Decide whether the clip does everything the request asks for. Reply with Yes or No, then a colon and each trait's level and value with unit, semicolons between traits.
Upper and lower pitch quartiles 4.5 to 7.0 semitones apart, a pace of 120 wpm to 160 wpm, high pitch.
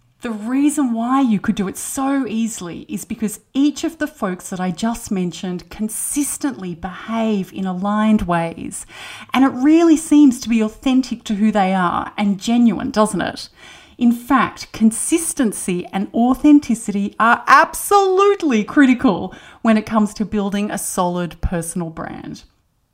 Yes: wide, 5.4 semitones; average, 145 wpm; high, 220 Hz